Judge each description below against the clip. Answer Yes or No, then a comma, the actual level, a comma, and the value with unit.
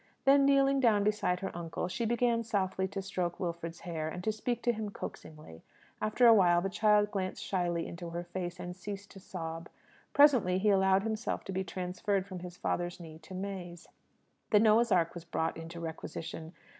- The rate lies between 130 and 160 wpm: No, average, 190 wpm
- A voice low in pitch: No, medium, 185 Hz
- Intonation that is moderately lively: Yes, average, 3.5 semitones